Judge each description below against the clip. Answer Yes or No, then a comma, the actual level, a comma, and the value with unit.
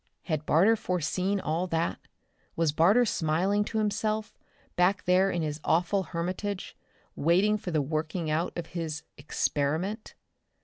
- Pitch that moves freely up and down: No, average, 3.9 semitones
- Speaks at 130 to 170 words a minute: Yes, slow, 135 wpm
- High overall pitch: No, medium, 175 Hz